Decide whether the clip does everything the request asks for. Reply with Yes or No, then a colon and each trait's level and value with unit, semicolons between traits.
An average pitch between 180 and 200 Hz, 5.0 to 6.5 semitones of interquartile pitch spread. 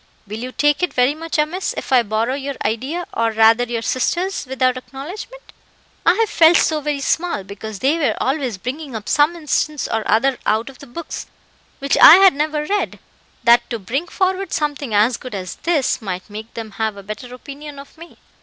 No: very high, 270 Hz; average, 5.3 semitones